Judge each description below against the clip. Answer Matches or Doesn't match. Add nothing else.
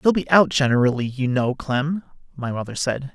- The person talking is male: Matches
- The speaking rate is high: Doesn't match